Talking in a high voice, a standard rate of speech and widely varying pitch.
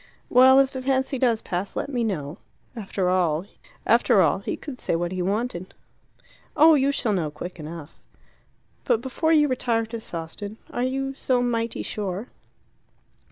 Yes: high, 230 Hz; average, 160 wpm; wide, 6.2 semitones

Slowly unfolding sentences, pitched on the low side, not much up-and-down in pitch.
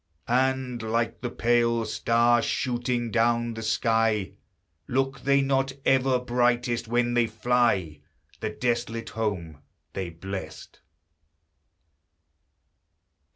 Yes: slow, 100 wpm; low, 120 Hz; narrow, 1.7 semitones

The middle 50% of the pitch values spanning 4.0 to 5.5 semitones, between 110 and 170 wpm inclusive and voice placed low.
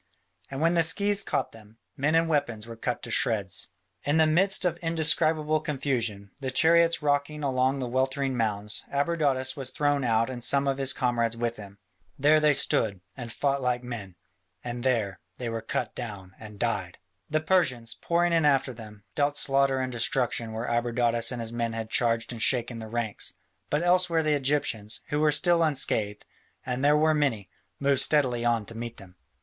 No: average, 4.4 semitones; average, 185 wpm; low, 130 Hz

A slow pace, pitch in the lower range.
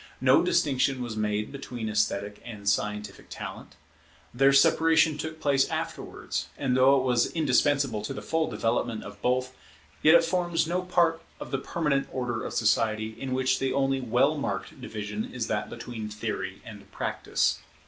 No: average, 165 wpm; low, 130 Hz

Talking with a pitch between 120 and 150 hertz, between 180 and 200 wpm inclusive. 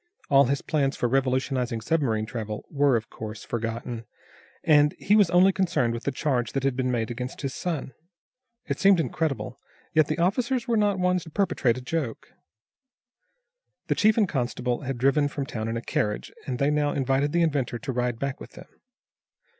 Yes: low, 135 Hz; average, 185 wpm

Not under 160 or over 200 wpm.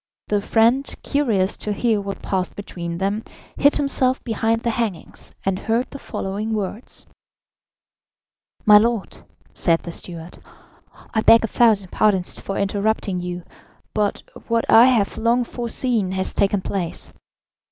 No: average, 140 wpm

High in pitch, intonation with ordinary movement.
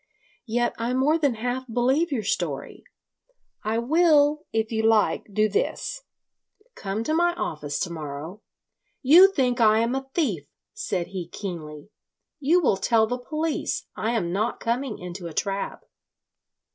No: high, 230 Hz; wide, 5.8 semitones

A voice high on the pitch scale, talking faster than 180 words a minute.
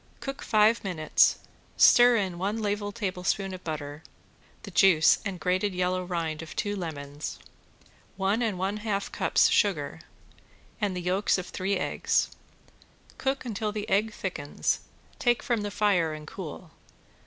No: high, 195 Hz; average, 150 wpm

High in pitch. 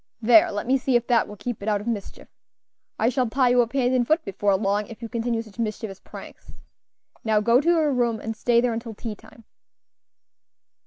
Yes: high, 230 Hz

